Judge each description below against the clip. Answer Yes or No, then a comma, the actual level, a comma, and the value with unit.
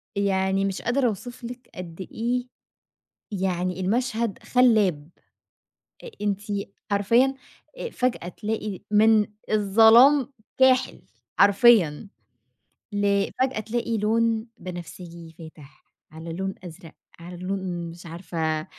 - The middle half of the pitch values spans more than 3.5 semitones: Yes, average, 4.5 semitones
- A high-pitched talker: Yes, high, 200 Hz